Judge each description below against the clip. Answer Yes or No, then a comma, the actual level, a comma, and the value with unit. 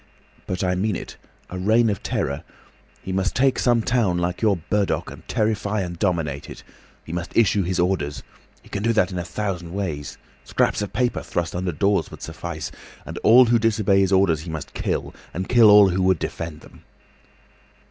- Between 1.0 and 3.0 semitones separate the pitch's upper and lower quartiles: No, average, 3.4 semitones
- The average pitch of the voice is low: Yes, very low, 95 Hz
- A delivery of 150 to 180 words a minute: No, average, 190 wpm